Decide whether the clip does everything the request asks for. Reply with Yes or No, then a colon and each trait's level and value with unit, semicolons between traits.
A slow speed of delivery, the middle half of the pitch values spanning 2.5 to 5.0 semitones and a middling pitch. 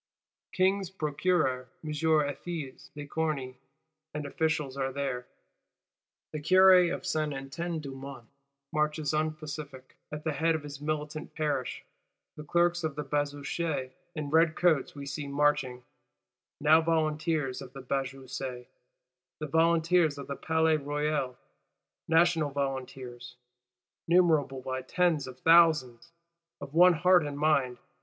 Yes: slow, 125 wpm; average, 2.9 semitones; medium, 150 Hz